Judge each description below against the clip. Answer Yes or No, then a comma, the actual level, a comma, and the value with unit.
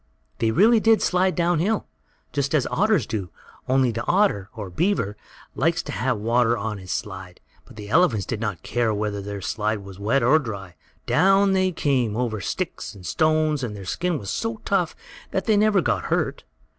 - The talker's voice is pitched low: Yes, low, 125 Hz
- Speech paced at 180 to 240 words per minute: Yes, average, 190 wpm